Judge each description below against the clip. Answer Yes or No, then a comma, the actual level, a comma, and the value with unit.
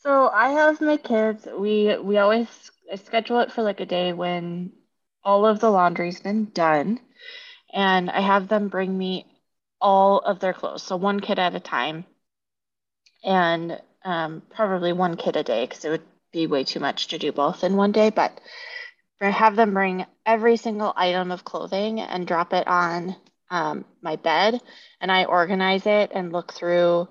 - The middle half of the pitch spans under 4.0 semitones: Yes, average, 3.6 semitones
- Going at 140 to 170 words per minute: No, average, 180 wpm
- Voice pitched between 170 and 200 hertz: Yes, high, 190 Hz